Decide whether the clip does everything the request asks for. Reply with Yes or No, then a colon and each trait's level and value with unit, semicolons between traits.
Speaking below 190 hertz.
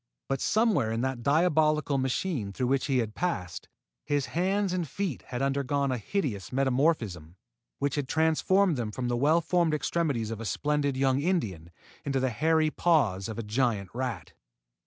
Yes: low, 135 Hz